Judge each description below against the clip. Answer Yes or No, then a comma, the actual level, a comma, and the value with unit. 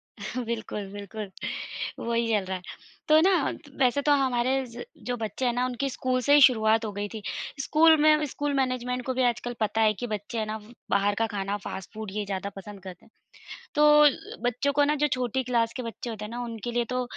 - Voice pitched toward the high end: Yes, high, 235 Hz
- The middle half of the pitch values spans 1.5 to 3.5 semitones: Yes, average, 3.2 semitones